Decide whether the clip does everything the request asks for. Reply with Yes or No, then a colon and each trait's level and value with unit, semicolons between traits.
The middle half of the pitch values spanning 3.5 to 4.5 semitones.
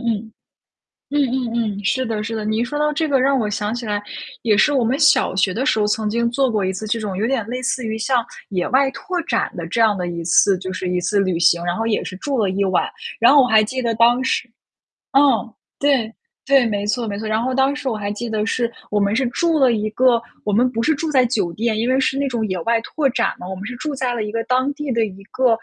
Yes: average, 3.8 semitones